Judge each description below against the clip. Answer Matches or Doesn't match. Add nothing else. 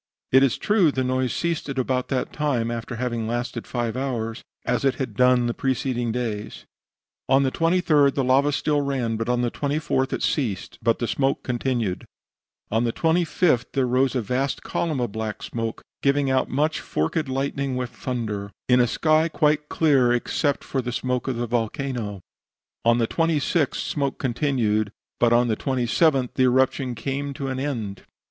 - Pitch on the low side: Matches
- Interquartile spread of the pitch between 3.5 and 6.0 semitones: Doesn't match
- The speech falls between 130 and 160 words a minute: Doesn't match